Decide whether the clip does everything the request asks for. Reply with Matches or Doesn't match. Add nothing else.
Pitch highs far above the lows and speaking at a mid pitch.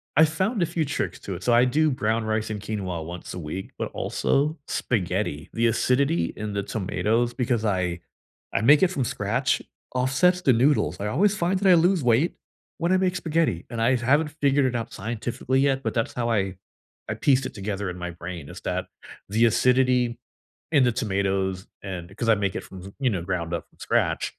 Doesn't match